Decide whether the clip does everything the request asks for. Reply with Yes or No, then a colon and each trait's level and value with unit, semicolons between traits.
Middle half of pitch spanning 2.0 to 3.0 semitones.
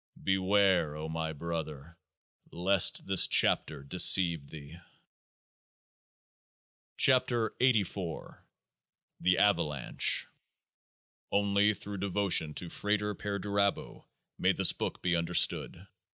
No: average, 3.9 semitones